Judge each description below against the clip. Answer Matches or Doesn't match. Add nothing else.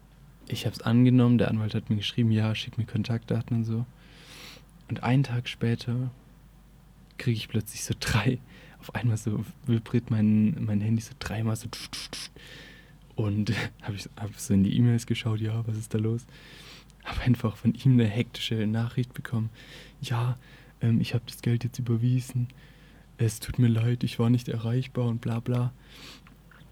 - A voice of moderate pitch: Doesn't match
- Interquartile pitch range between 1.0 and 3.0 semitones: Matches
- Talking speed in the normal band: Matches